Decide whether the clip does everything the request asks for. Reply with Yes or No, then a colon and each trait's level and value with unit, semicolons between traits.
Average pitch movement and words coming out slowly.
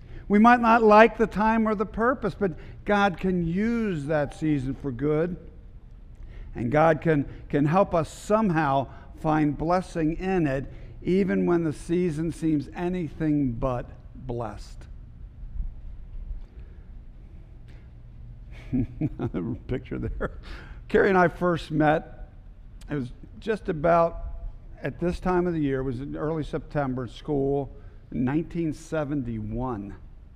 No: wide, 5.8 semitones; slow, 120 wpm